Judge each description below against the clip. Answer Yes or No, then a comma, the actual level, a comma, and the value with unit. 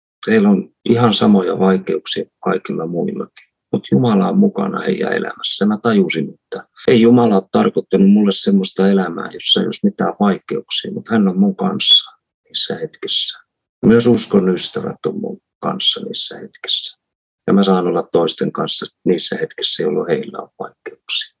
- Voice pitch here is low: Yes, low, 120 Hz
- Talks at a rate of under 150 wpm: No, fast, 155 wpm